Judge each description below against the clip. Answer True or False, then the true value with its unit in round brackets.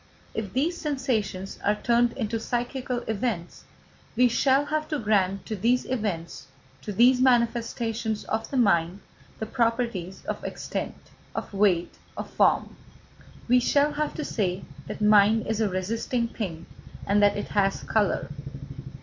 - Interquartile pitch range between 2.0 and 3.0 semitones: False (3.7 semitones)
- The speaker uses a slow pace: False (145 wpm)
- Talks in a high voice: True (225 Hz)